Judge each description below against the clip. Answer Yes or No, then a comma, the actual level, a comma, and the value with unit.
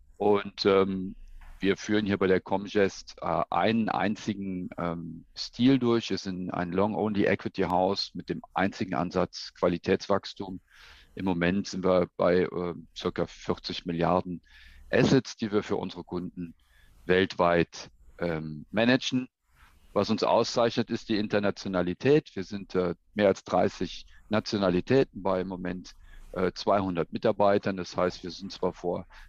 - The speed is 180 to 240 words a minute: No, average, 135 wpm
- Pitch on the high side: No, very low, 95 Hz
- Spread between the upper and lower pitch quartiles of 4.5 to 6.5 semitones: No, average, 2.7 semitones